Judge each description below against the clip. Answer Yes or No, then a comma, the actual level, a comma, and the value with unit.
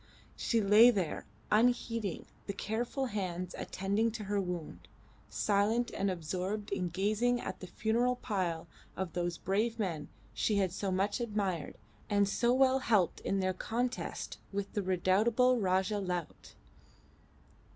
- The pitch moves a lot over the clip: No, average, 3.6 semitones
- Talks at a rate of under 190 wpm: Yes, average, 140 wpm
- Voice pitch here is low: No, high, 200 Hz